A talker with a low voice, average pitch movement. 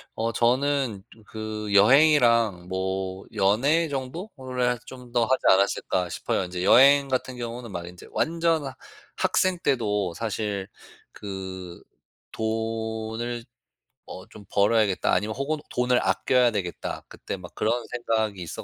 Yes: low, 115 Hz; average, 4.3 semitones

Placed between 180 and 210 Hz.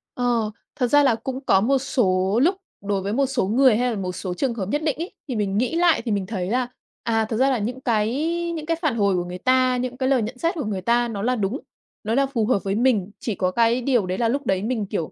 No: high, 235 Hz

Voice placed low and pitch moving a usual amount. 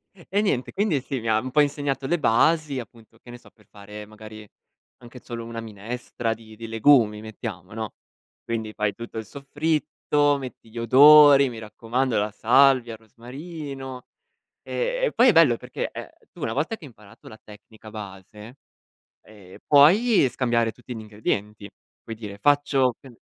Yes: low, 120 Hz; average, 4.4 semitones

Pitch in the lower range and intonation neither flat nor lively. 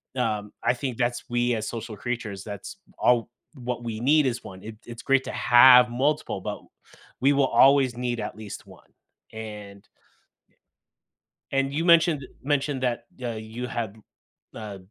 Yes: low, 120 Hz; average, 3.4 semitones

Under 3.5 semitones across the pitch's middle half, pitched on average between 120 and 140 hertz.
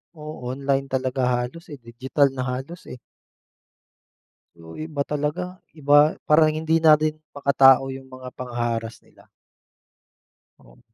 Yes: average, 3.0 semitones; low, 135 Hz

